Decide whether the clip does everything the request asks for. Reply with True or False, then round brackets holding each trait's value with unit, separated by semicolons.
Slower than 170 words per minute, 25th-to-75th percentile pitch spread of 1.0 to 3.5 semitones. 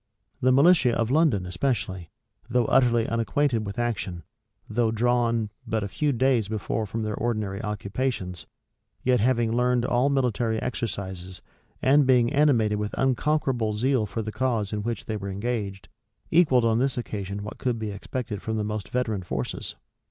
True (160 wpm; 3.2 semitones)